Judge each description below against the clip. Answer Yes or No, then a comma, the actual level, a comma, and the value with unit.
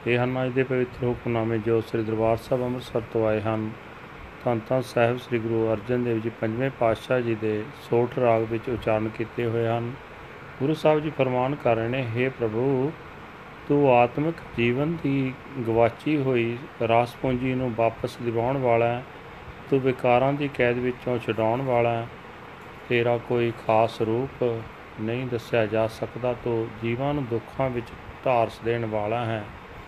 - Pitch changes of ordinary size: No, narrow, 2.2 semitones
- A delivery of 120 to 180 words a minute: Yes, average, 160 wpm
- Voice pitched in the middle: No, low, 120 Hz